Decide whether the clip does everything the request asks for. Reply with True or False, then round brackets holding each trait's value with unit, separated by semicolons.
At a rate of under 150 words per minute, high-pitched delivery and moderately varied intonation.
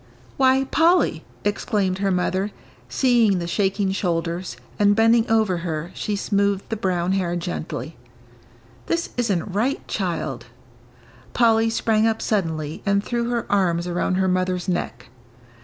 True (140 wpm; 195 Hz; 4.2 semitones)